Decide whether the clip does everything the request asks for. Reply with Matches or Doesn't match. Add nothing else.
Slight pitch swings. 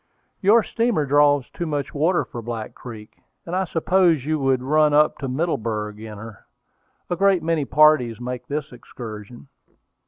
Doesn't match